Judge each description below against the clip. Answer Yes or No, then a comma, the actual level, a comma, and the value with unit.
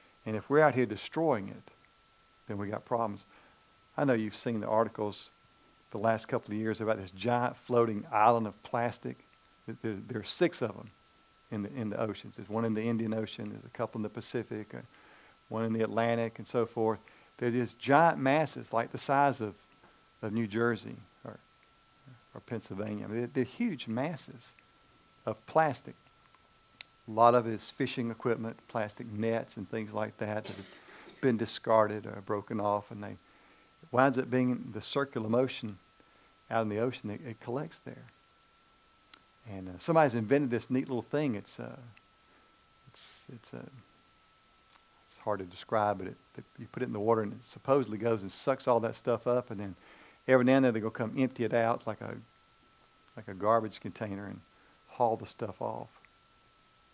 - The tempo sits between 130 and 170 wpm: No, average, 185 wpm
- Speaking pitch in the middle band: No, low, 115 Hz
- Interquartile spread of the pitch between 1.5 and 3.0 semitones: Yes, narrow, 2.6 semitones